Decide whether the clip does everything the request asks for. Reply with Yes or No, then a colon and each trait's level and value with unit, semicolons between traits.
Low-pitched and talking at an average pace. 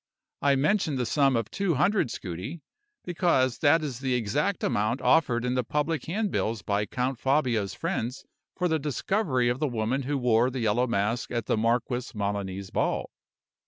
Yes: low, 125 Hz; average, 170 wpm